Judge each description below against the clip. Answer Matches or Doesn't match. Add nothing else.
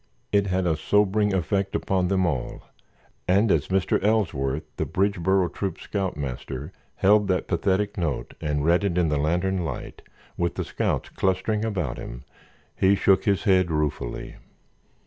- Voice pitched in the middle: Doesn't match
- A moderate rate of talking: Matches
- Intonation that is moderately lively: Matches